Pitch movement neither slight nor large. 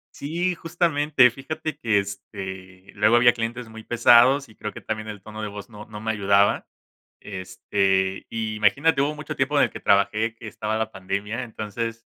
Yes: average, 3.7 semitones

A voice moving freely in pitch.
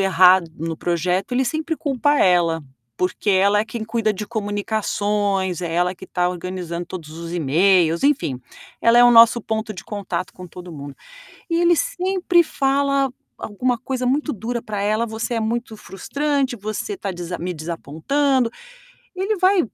Yes: wide, 6.3 semitones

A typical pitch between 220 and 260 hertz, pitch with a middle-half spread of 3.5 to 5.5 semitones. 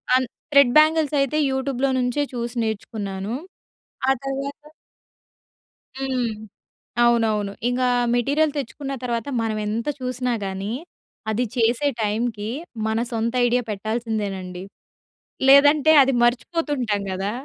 Yes: high, 240 Hz; average, 3.9 semitones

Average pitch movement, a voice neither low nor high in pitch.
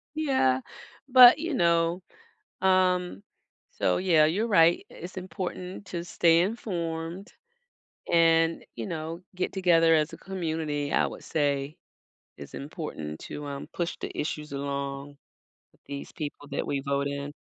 Yes: average, 4.1 semitones; medium, 165 Hz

